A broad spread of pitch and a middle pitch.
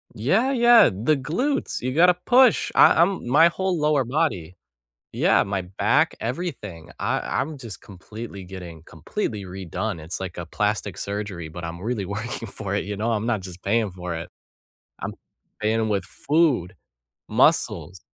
No: wide, 8.2 semitones; low, 105 Hz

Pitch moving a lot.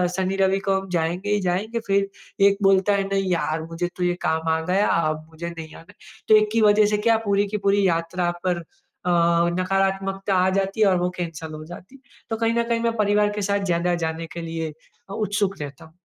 No: average, 3.1 semitones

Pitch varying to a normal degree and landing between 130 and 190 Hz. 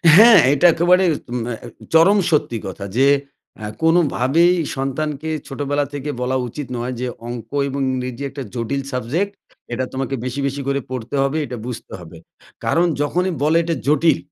Yes: average, 4.1 semitones; medium, 140 Hz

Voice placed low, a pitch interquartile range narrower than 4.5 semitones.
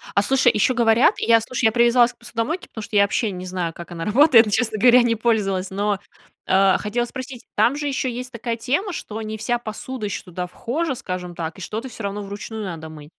No: high, 220 Hz; average, 3.8 semitones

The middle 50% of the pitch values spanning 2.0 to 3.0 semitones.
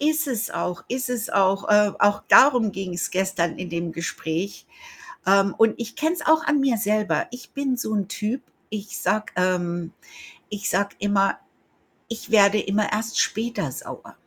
No: average, 3.7 semitones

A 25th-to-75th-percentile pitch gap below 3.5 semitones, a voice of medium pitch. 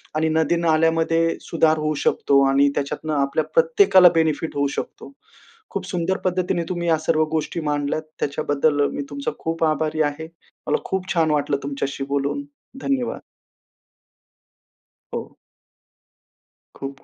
Yes: narrow, 2.6 semitones; medium, 155 Hz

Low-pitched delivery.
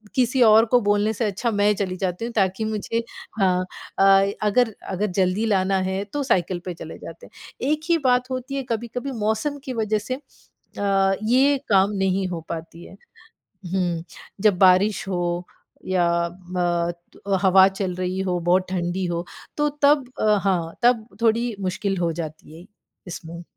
No: high, 195 Hz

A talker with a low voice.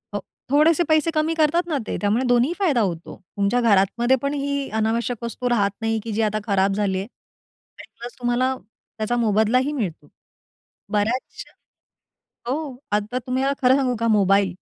No: high, 240 Hz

